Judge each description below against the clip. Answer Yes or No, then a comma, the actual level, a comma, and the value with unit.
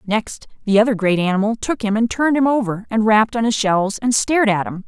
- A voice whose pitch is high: Yes, high, 220 Hz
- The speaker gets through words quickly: Yes, fast, 245 wpm